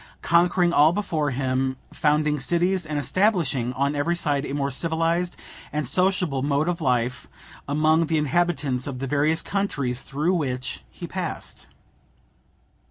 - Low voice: No, medium, 150 Hz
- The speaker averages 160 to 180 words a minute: No, average, 140 wpm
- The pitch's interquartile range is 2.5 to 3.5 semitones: No, average, 3.9 semitones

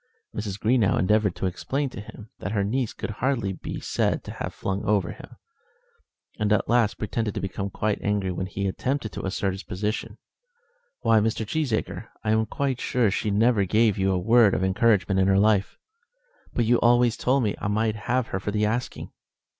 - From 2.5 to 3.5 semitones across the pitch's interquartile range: Yes, average, 2.9 semitones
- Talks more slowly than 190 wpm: No, average, 195 wpm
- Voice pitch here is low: Yes, low, 105 Hz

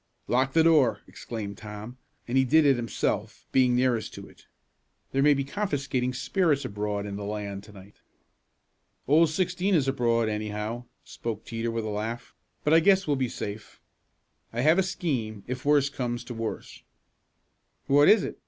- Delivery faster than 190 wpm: No, average, 170 wpm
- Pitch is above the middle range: No, low, 125 Hz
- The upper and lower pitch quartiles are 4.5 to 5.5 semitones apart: Yes, average, 5.0 semitones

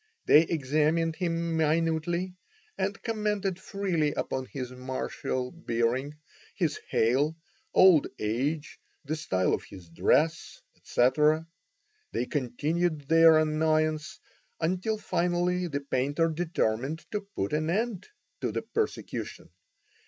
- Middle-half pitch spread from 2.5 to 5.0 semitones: Yes, average, 4.0 semitones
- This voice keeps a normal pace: No, slow, 110 wpm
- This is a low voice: No, medium, 155 Hz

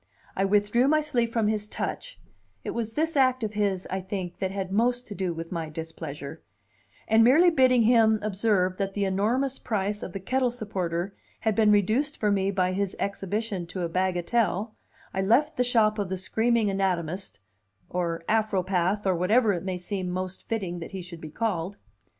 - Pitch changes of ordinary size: Yes, average, 3.6 semitones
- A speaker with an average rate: Yes, average, 185 wpm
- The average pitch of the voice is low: No, high, 200 Hz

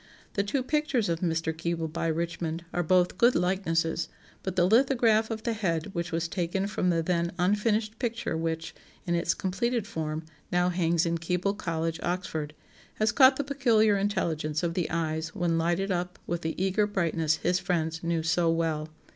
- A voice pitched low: No, medium, 175 Hz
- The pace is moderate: Yes, average, 180 wpm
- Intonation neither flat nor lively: Yes, average, 3.8 semitones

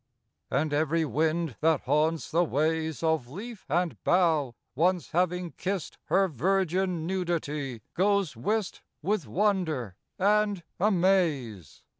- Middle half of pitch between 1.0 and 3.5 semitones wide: No, average, 4.0 semitones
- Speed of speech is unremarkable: No, slow, 115 wpm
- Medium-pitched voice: Yes, medium, 165 Hz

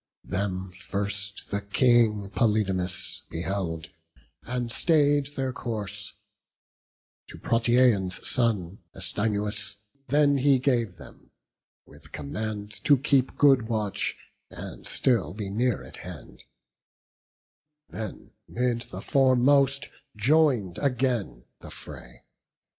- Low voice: Yes, low, 110 Hz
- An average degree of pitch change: Yes, average, 4.4 semitones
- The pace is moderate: No, slow, 100 wpm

